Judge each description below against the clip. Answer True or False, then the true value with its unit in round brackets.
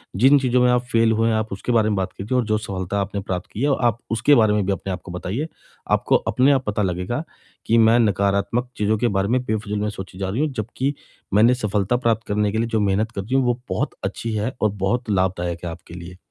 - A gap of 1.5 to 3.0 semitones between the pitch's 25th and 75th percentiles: False (3.5 semitones)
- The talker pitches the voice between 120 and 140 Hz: False (110 Hz)